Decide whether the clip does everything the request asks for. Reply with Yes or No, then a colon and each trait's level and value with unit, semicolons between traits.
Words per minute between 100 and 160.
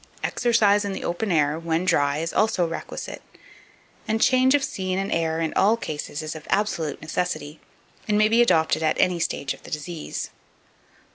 No: average, 180 wpm